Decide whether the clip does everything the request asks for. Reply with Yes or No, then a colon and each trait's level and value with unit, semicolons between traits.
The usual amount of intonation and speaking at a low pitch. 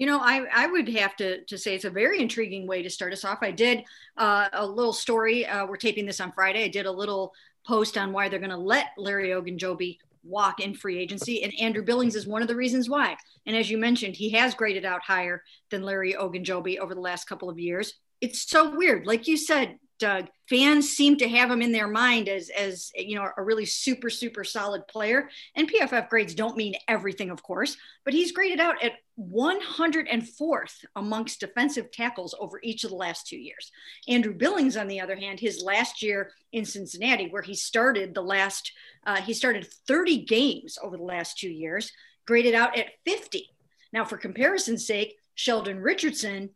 No: average, 3.8 semitones; high, 220 Hz